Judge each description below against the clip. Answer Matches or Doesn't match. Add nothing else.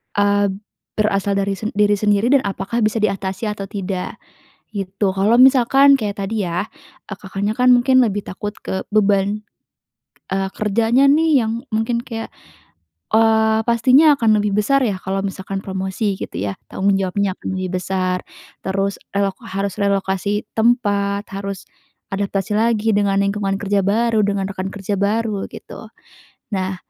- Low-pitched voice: Doesn't match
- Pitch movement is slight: Matches